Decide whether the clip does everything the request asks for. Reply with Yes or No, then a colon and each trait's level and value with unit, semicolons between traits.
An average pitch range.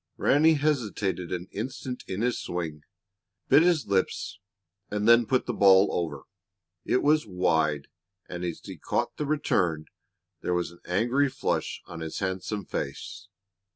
No: wide, 6.5 semitones